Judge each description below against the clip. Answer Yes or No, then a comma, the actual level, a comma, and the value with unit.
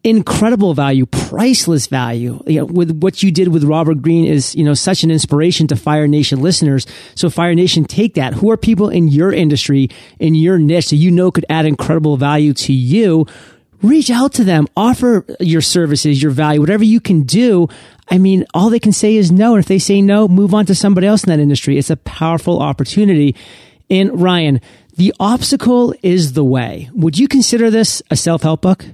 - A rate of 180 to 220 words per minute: Yes, fast, 205 wpm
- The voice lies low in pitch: No, medium, 170 Hz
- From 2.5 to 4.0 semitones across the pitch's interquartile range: No, average, 5.1 semitones